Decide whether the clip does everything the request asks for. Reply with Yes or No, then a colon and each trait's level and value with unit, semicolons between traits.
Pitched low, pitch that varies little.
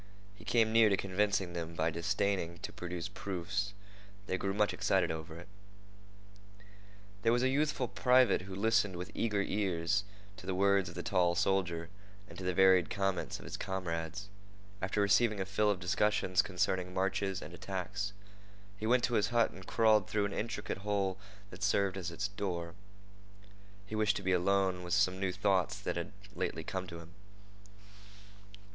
Yes: very low, 95 Hz; narrow, 2.3 semitones